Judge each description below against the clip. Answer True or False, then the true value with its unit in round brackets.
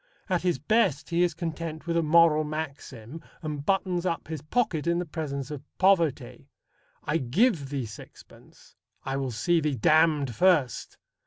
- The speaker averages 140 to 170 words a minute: True (160 wpm)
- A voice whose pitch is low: False (155 Hz)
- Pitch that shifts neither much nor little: True (3.4 semitones)